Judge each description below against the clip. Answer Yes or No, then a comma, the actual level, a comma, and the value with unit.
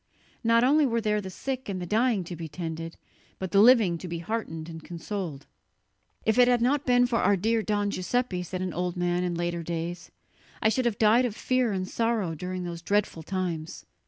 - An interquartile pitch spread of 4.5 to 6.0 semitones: Yes, average, 5.0 semitones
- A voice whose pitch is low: No, high, 190 Hz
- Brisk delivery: Yes, fast, 210 wpm